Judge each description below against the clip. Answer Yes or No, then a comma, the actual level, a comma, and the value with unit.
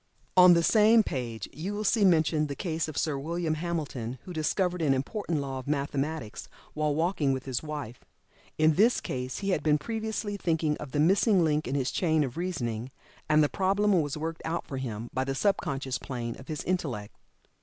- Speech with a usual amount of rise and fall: Yes, average, 4.7 semitones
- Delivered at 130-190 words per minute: No, average, 200 wpm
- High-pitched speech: No, medium, 155 Hz